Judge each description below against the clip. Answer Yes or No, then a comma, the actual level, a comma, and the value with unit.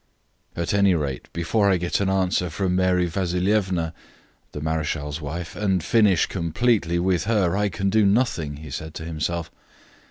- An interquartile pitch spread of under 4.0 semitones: Yes, average, 3.2 semitones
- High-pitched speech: No, very low, 90 Hz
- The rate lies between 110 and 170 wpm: Yes, average, 160 wpm